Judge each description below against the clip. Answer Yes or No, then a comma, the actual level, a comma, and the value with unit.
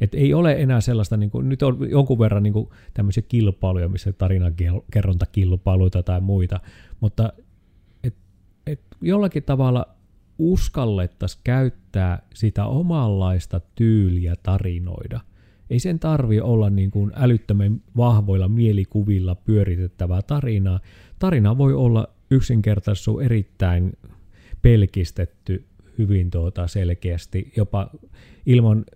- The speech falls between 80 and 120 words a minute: Yes, average, 110 wpm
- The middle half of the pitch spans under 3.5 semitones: No, average, 4.0 semitones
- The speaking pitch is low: Yes, low, 100 Hz